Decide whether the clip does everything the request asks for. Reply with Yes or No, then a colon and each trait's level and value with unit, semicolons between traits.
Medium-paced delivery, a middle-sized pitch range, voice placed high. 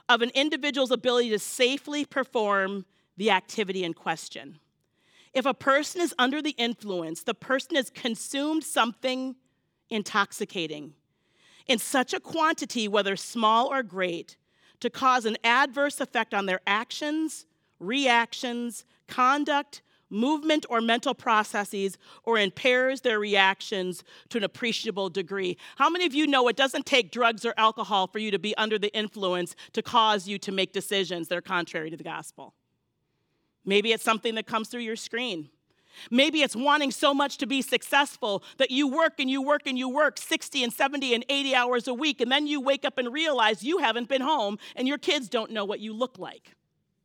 Yes: average, 175 wpm; average, 4.9 semitones; high, 235 Hz